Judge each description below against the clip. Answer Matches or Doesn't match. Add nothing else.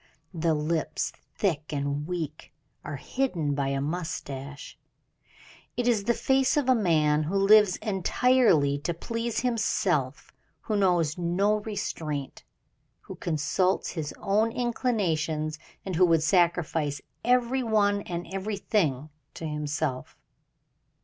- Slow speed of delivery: Matches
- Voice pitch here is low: Doesn't match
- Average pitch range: Doesn't match